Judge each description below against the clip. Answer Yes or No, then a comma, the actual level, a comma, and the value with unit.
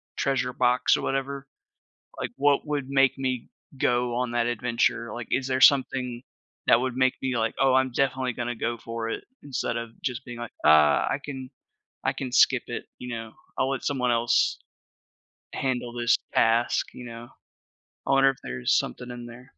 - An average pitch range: No, narrow, 1.9 semitones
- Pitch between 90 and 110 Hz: No, low, 125 Hz